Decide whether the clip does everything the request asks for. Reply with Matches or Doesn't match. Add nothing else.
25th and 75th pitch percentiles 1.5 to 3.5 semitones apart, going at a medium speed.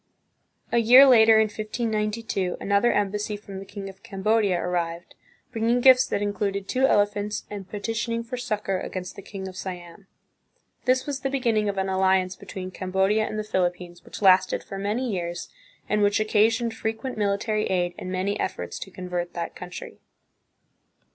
Matches